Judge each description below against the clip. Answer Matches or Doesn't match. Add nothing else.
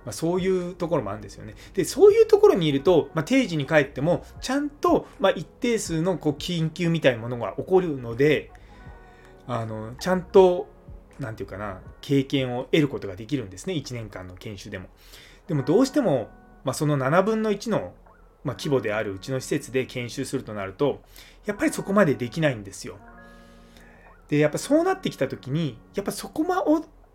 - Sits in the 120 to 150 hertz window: Matches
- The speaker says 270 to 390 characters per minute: Matches